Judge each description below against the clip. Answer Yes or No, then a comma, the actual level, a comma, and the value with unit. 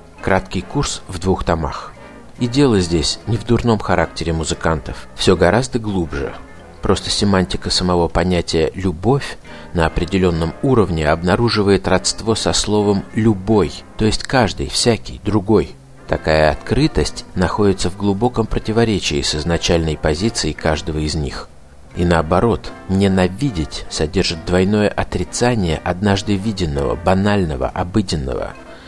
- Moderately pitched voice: No, very low, 90 Hz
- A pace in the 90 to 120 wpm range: Yes, average, 115 wpm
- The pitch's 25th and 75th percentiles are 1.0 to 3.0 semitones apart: No, average, 4.3 semitones